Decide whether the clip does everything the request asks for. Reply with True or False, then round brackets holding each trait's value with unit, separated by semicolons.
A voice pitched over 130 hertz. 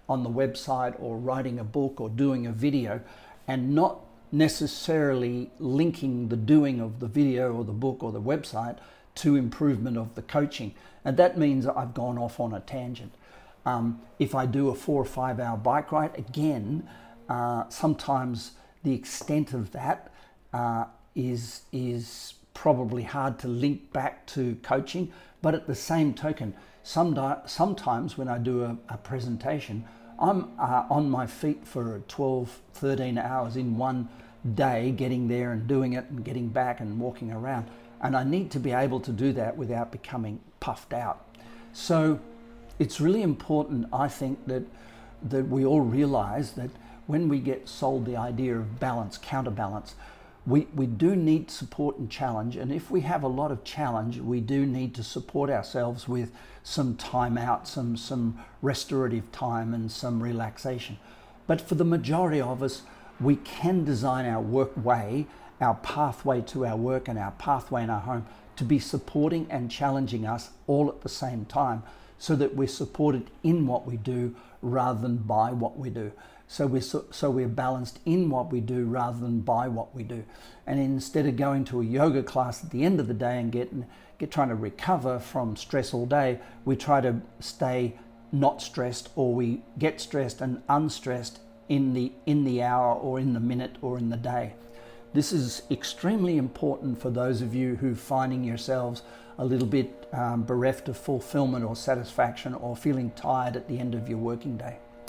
False (125 Hz)